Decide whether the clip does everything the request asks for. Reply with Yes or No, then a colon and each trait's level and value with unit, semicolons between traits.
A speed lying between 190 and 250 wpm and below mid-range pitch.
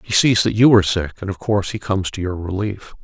No: fast, 275 wpm; low, 100 Hz